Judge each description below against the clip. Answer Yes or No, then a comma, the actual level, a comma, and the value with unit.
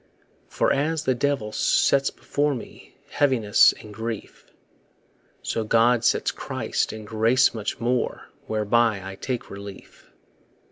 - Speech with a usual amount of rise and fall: Yes, average, 3.3 semitones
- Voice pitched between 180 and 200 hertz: No, low, 115 Hz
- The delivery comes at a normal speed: No, slow, 125 wpm